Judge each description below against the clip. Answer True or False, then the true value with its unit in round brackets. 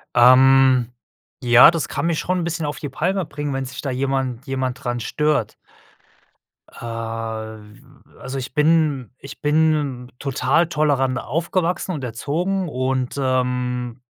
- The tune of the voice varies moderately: True (3.5 semitones)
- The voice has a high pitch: False (135 Hz)